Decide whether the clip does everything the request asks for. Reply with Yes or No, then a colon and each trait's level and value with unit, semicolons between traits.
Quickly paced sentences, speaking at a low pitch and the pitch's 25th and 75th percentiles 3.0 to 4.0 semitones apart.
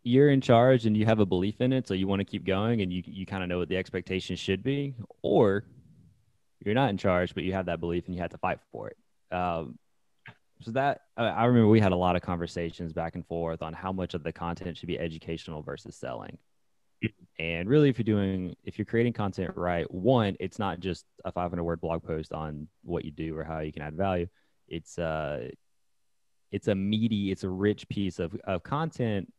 Yes: fast, 225 wpm; very low, 95 Hz; average, 3.6 semitones